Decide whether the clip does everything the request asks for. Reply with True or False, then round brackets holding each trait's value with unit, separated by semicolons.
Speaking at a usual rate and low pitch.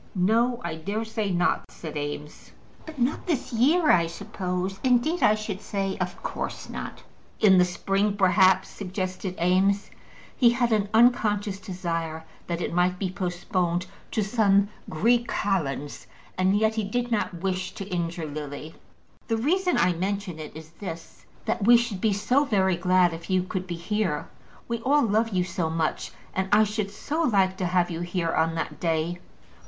False (175 wpm; 190 Hz)